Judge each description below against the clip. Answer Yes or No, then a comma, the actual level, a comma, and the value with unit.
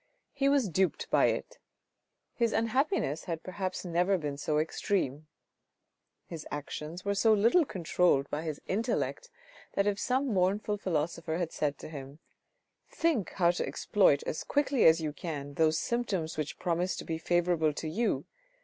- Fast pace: No, average, 160 wpm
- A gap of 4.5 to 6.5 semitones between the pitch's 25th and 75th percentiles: Yes, average, 4.9 semitones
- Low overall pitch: No, medium, 175 Hz